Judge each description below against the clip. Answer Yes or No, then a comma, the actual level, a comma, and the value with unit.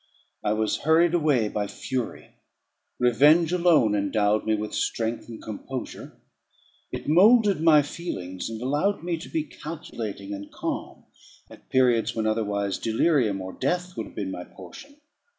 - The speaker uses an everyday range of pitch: No, wide, 7.7 semitones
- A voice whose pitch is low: Yes, low, 120 Hz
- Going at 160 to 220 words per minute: No, average, 150 wpm